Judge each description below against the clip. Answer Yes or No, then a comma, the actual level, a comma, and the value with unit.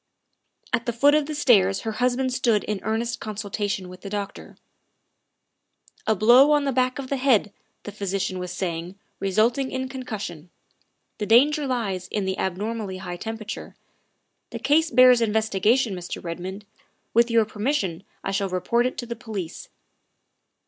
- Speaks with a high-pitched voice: Yes, high, 220 Hz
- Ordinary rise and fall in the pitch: Yes, average, 4.7 semitones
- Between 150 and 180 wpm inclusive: Yes, average, 165 wpm